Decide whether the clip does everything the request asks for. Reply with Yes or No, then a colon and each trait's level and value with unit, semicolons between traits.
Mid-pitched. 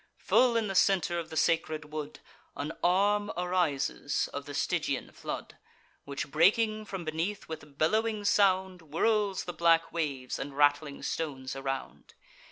Yes: medium, 165 Hz